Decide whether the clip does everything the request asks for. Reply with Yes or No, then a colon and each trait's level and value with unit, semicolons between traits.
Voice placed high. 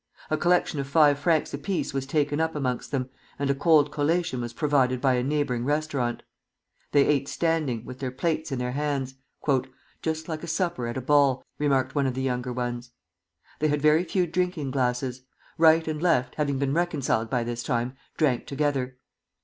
No: medium, 140 Hz